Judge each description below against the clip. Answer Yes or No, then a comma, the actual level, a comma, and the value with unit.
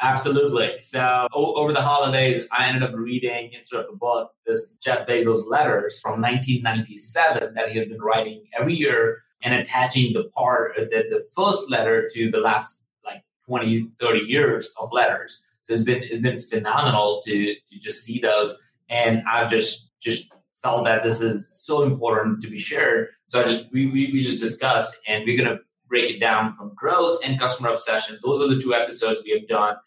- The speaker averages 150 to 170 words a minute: No, average, 190 wpm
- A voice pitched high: No, low, 120 Hz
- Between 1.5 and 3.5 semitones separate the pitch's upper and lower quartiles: Yes, average, 3.2 semitones